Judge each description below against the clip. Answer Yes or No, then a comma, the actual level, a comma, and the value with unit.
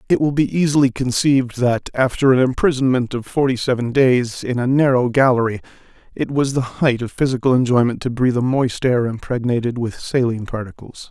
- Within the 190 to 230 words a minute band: No, average, 180 wpm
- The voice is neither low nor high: No, low, 125 Hz